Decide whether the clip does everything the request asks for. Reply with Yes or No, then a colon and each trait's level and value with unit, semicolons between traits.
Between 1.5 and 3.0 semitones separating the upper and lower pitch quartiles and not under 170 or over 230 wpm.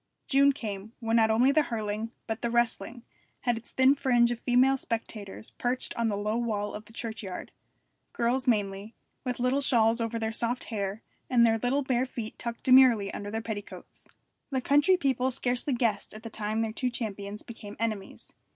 Yes: average, 2.7 semitones; average, 185 wpm